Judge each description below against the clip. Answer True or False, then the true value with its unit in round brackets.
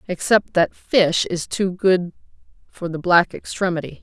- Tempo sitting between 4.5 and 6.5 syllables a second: False (4.3 syllables/s)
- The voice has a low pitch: False (180 Hz)